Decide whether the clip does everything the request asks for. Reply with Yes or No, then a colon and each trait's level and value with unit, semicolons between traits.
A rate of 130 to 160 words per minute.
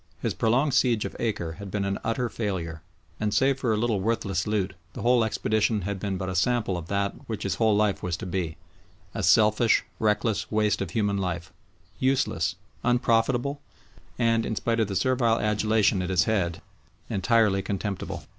No: average, 180 wpm